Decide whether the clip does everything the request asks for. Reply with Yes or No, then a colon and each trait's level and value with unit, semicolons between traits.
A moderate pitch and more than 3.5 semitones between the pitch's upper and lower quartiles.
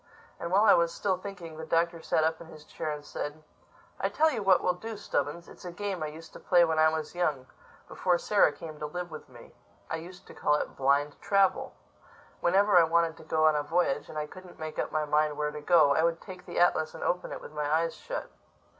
No: medium, 165 Hz; average, 2.7 semitones